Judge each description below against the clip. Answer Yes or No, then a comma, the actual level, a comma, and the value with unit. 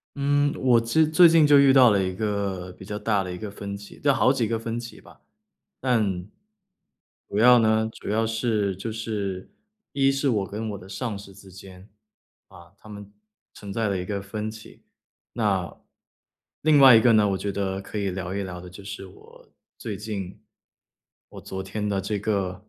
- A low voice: Yes, low, 105 Hz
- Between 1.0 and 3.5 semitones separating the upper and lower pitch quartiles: Yes, average, 3.0 semitones